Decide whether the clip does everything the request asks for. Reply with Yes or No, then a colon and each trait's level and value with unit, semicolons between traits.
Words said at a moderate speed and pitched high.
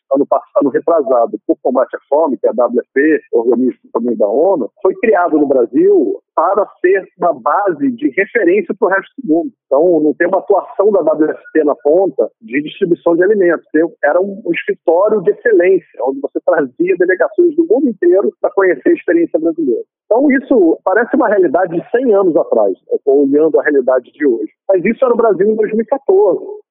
No: fast, 190 wpm; very high, 270 Hz